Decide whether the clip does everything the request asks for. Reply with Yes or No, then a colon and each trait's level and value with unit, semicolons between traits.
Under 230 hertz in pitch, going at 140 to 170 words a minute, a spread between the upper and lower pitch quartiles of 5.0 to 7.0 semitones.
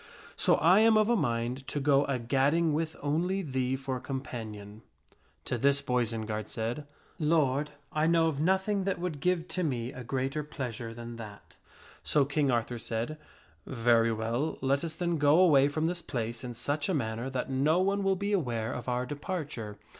No: medium, 140 Hz; average, 190 wpm; average, 5.3 semitones